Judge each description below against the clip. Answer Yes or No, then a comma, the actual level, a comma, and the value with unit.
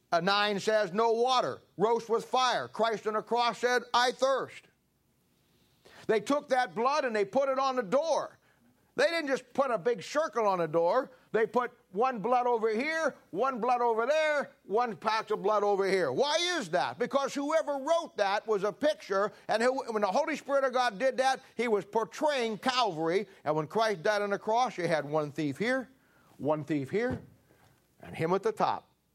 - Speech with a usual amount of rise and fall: Yes, average, 4.2 semitones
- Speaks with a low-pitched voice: No, high, 235 Hz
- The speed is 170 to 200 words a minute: Yes, average, 195 wpm